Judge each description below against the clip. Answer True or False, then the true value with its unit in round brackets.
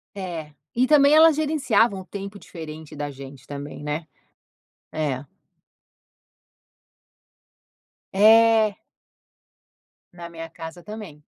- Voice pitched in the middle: True (175 Hz)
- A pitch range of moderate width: False (6.6 semitones)